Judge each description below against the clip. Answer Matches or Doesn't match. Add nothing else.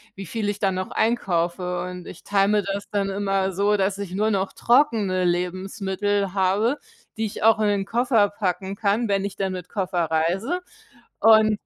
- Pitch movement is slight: Matches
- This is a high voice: Matches